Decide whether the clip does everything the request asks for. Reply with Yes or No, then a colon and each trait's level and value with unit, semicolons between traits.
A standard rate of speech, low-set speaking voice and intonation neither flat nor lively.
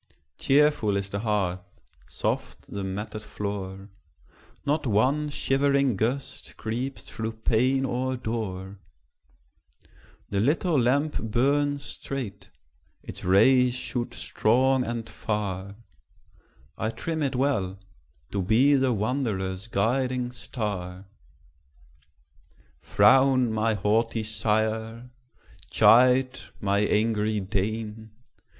No: slow, 95 wpm; low, 115 Hz; average, 4.2 semitones